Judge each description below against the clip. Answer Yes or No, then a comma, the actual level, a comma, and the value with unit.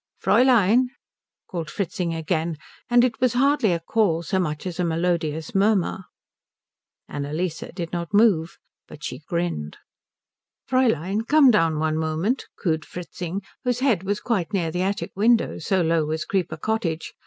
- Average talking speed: Yes, average, 150 wpm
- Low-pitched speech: No, medium, 180 Hz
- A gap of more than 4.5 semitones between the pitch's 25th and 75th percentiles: Yes, average, 5.2 semitones